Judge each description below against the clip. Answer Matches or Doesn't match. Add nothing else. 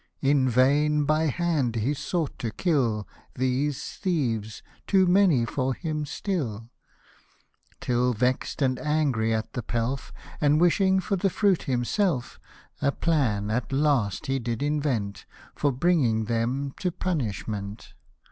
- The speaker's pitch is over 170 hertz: Doesn't match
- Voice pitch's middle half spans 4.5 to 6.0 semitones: Matches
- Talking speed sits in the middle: Doesn't match